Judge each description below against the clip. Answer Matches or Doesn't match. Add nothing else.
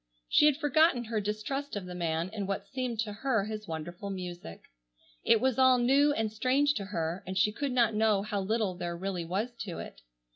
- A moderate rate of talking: Doesn't match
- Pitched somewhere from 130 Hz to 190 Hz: Doesn't match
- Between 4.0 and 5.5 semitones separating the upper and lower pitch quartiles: Matches